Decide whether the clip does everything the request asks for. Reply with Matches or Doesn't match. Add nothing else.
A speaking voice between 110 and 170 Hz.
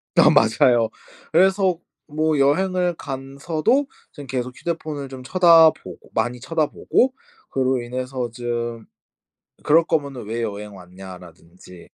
Matches